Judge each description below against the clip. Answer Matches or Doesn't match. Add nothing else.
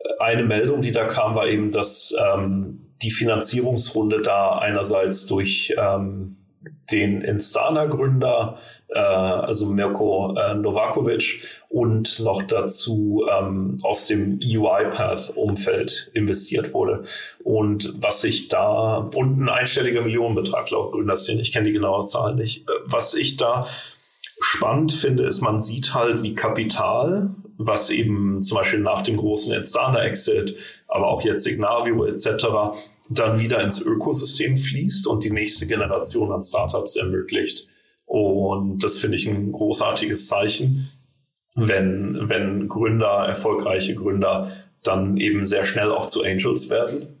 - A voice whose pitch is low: Matches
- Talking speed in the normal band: Matches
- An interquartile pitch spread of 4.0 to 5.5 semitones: Doesn't match